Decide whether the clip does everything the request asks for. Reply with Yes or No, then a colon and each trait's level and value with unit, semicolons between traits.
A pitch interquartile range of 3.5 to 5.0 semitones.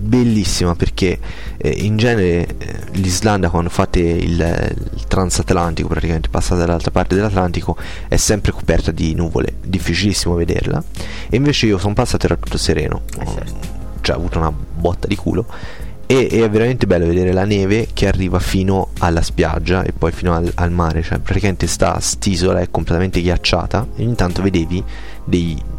No: average, 2.7 semitones